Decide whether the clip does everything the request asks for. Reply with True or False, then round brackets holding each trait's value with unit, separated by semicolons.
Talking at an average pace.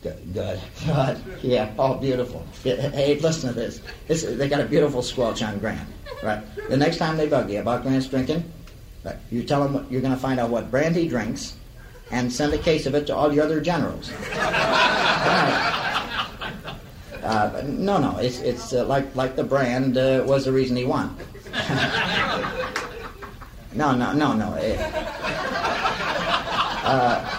True (165 wpm)